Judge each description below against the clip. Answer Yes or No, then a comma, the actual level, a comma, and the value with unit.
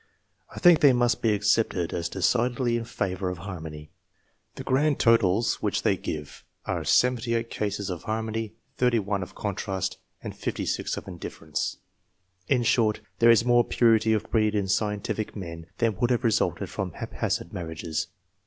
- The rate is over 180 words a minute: No, average, 155 wpm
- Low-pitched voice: Yes, low, 110 Hz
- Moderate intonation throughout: Yes, average, 4.0 semitones